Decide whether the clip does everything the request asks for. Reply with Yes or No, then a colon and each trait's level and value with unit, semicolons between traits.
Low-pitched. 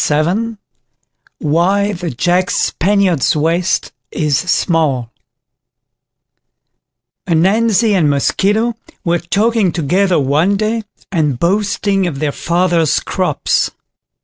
No: medium, 175 Hz